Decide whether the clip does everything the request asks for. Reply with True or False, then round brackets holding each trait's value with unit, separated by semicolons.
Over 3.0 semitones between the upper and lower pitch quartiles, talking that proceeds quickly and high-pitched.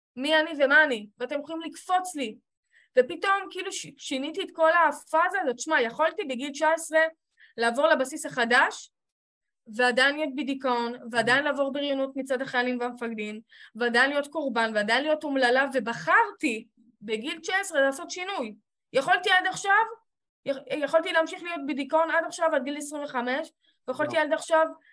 False (4.5 semitones; 140 wpm; 290 Hz)